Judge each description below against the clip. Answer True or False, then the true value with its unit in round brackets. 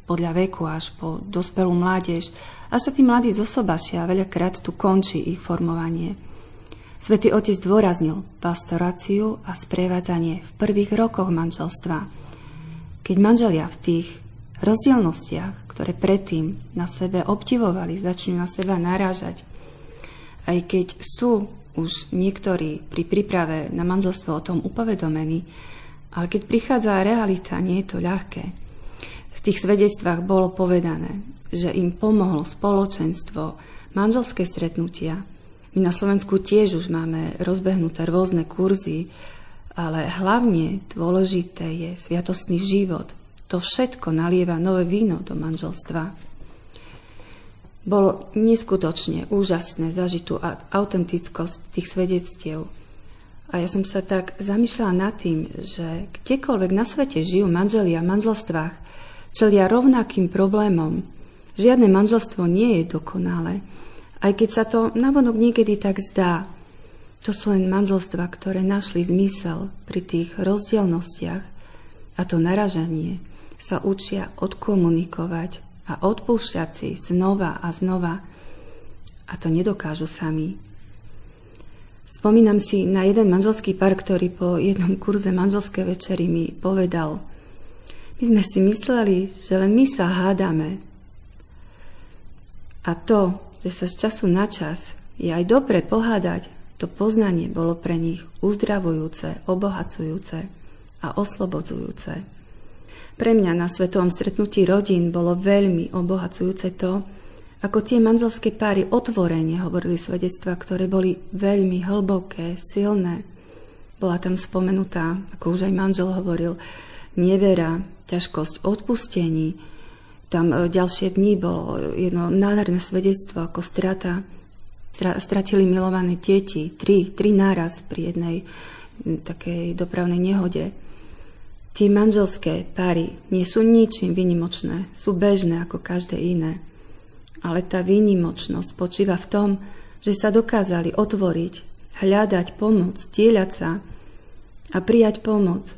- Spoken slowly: False (120 wpm)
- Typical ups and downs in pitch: True (3.0 semitones)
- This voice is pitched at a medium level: True (180 Hz)